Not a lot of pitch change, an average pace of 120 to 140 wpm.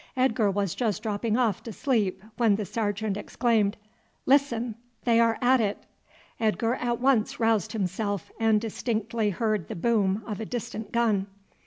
No: narrow, 2.3 semitones; average, 155 wpm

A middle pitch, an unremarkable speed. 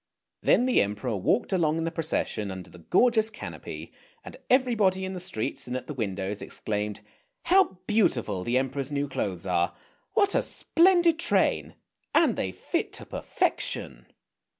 Yes: medium, 150 Hz; average, 155 wpm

